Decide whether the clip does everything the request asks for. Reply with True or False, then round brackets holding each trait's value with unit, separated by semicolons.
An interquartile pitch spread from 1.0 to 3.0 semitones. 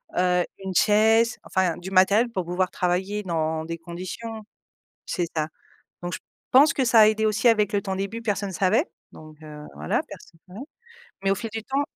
False (3.9 semitones)